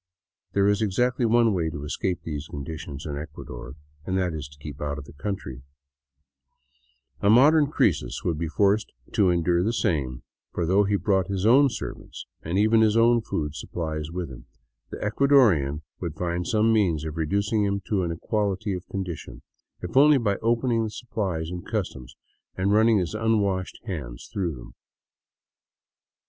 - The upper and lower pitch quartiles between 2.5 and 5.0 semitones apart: No, wide, 5.5 semitones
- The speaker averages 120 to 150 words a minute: No, average, 165 wpm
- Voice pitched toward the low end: Yes, very low, 95 Hz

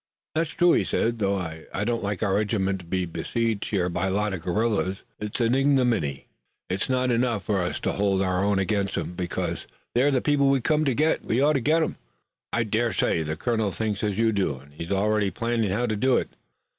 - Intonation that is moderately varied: Yes, average, 4.1 semitones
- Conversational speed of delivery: No, fast, 230 wpm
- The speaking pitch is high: No, low, 105 Hz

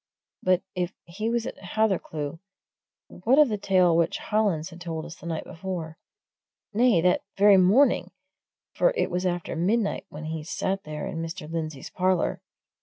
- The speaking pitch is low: No, medium, 180 Hz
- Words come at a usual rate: Yes, average, 165 wpm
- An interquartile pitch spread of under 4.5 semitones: Yes, average, 3.8 semitones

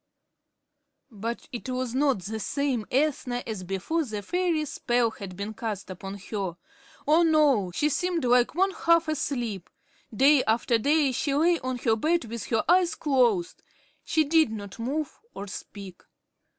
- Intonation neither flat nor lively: No, wide, 6.1 semitones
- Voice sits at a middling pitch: No, very high, 250 Hz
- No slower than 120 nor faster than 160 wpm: Yes, average, 155 wpm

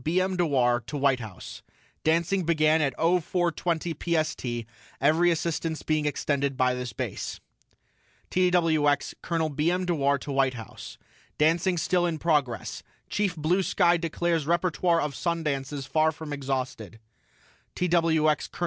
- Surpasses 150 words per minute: No, average, 145 wpm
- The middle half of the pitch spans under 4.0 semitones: Yes, average, 3.5 semitones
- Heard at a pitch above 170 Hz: No, medium, 155 Hz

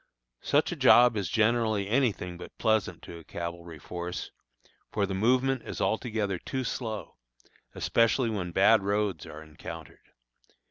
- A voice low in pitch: Yes, low, 105 Hz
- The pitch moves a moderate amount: Yes, average, 4.6 semitones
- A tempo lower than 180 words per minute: Yes, average, 145 wpm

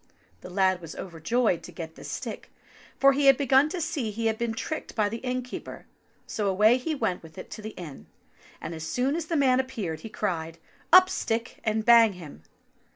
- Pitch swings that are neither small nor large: No, wide, 6.3 semitones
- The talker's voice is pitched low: No, high, 225 Hz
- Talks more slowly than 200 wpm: No, fast, 205 wpm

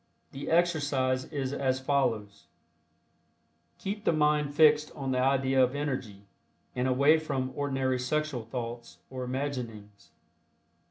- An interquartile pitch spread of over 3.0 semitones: No, narrow, 2.5 semitones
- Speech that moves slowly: Yes, slow, 120 wpm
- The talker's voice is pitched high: No, low, 135 Hz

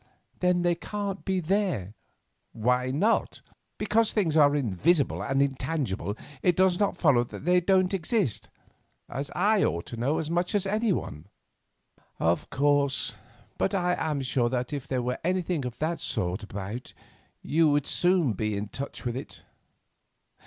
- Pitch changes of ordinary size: No, wide, 6.4 semitones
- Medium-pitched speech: Yes, medium, 150 Hz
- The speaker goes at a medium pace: Yes, average, 155 wpm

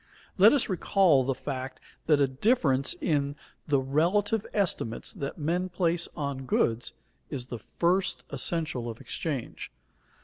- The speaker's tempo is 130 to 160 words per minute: Yes, average, 140 wpm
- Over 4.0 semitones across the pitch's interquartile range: Yes, average, 5.2 semitones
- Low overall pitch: No, medium, 150 Hz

